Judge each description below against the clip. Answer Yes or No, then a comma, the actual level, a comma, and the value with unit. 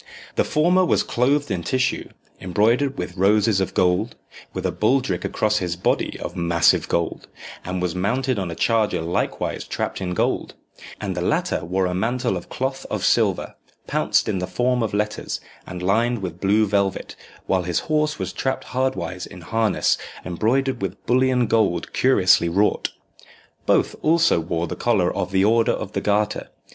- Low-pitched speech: Yes, low, 105 Hz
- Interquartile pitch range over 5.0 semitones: Yes, wide, 5.4 semitones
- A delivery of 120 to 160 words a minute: No, average, 170 wpm